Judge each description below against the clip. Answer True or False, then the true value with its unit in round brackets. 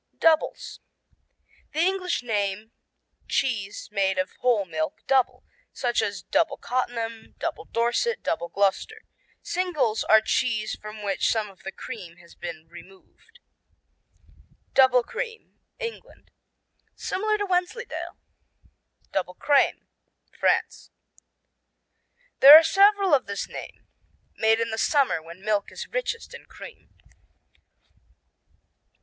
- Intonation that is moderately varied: False (8.5 semitones)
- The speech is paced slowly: True (115 wpm)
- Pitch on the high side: True (230 Hz)